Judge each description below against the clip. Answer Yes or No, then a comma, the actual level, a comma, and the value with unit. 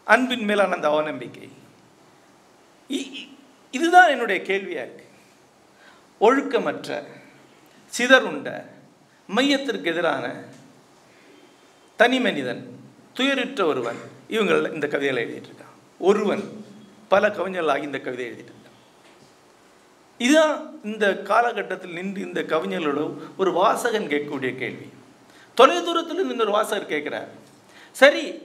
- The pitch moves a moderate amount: No, wide, 7.2 semitones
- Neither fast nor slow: Yes, average, 95 wpm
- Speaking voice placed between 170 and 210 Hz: No, high, 235 Hz